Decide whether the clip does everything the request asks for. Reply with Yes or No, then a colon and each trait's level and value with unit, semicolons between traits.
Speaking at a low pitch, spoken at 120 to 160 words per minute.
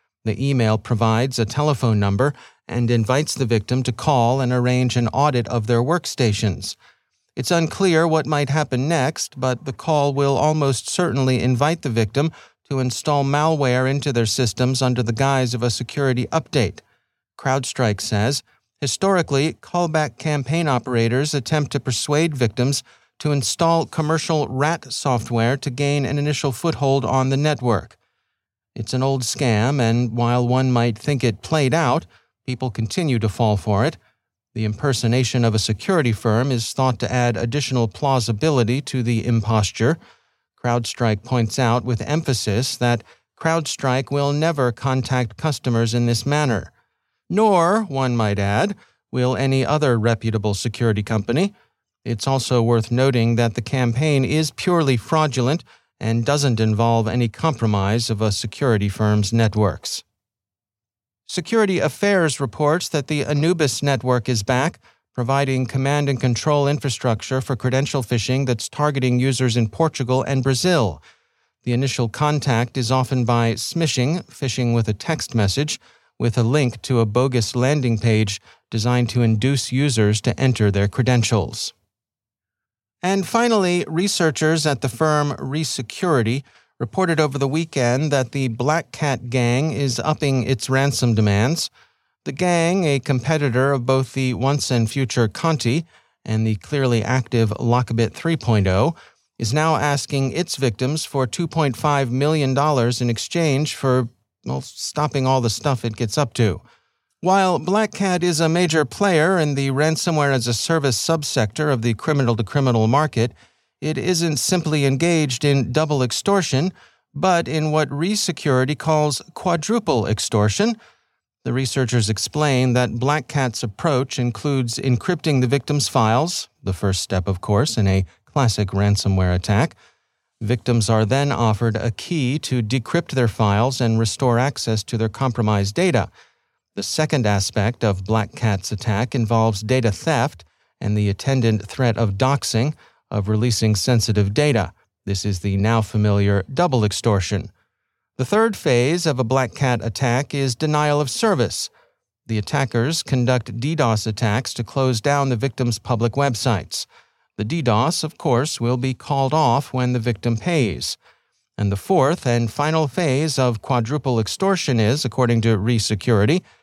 Yes: low, 130 Hz; average, 145 wpm